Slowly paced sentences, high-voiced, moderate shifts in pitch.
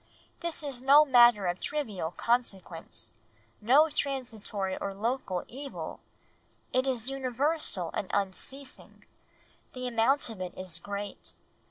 No: slow, 120 wpm; high, 240 Hz; wide, 5.8 semitones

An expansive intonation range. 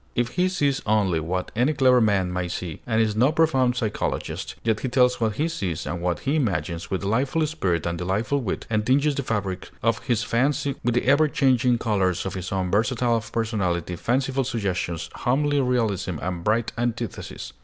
Yes: wide, 5.7 semitones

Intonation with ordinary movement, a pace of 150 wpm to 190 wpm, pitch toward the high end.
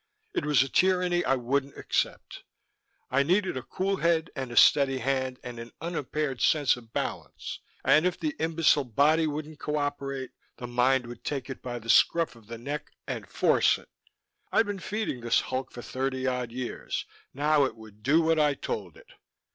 No: average, 3.9 semitones; average, 185 wpm; low, 135 Hz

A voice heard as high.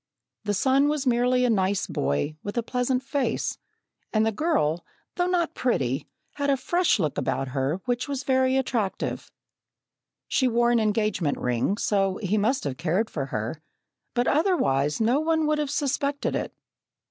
Yes: high, 235 Hz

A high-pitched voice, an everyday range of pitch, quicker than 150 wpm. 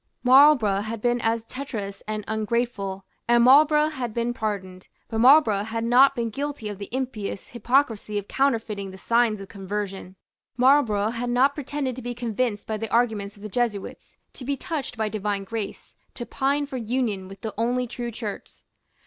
Yes: high, 230 Hz; average, 3.5 semitones; average, 175 wpm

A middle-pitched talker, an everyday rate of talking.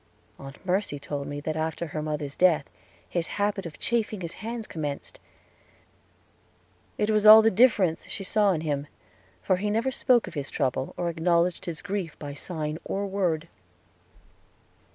Yes: medium, 175 Hz; average, 160 wpm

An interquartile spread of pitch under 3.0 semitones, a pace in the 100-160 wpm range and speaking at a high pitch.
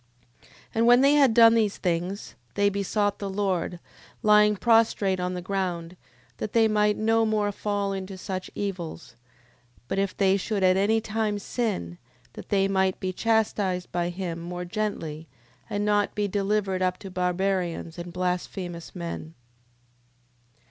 Yes: narrow, 2.6 semitones; average, 155 wpm; high, 195 Hz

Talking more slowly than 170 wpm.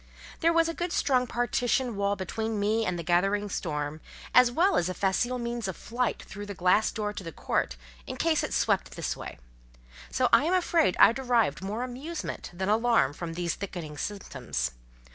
No: average, 190 wpm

